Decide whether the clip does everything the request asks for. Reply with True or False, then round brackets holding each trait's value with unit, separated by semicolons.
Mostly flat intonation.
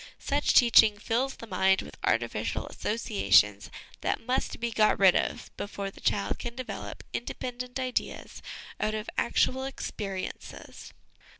False (4.0 semitones)